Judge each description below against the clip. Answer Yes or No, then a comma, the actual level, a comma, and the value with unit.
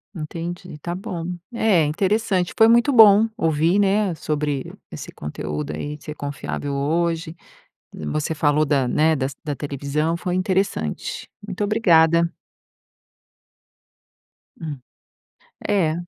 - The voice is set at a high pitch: No, medium, 160 Hz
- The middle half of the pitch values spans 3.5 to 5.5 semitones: Yes, average, 4.5 semitones